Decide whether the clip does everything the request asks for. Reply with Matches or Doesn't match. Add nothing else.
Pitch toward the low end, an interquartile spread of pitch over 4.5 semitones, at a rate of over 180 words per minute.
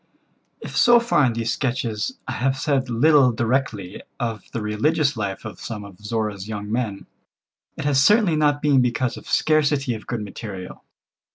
Doesn't match